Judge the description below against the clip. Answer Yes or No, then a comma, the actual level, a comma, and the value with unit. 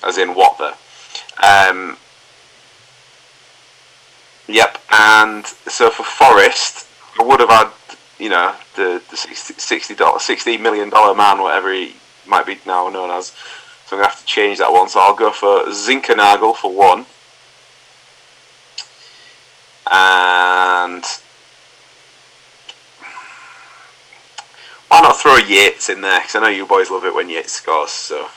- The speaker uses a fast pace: No, slow, 135 wpm